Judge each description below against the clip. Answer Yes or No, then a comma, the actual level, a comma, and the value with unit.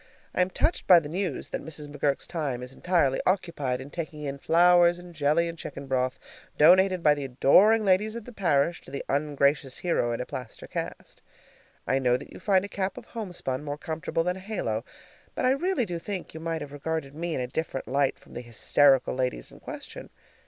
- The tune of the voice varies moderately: Yes, average, 4.8 semitones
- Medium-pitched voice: Yes, medium, 155 Hz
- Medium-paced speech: No, fast, 215 wpm